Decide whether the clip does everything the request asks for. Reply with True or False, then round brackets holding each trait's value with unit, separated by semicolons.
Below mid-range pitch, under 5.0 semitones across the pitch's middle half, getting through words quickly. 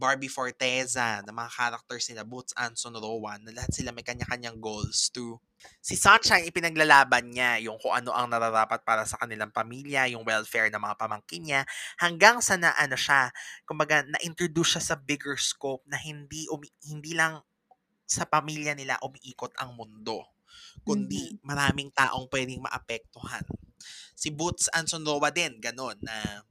True (130 Hz; 4.5 semitones; 160 wpm)